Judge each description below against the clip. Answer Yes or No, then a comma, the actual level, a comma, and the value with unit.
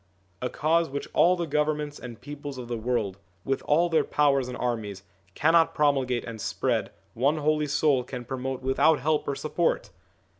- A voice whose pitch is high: No, medium, 140 Hz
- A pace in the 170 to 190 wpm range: Yes, average, 175 wpm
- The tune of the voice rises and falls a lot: No, average, 3.4 semitones